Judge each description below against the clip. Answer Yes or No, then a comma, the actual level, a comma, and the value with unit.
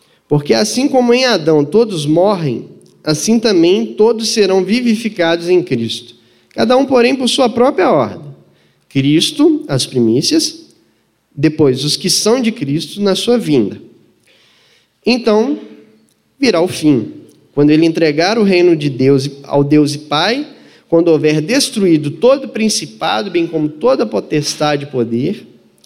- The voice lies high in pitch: No, medium, 175 Hz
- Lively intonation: Yes, wide, 8.2 semitones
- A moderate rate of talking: Yes, average, 140 wpm